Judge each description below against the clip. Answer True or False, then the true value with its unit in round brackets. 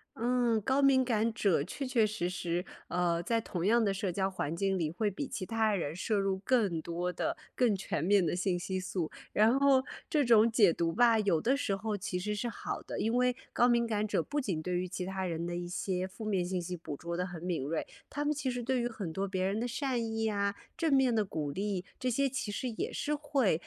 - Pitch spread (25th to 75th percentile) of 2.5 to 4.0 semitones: False (4.9 semitones)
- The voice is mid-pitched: False (205 Hz)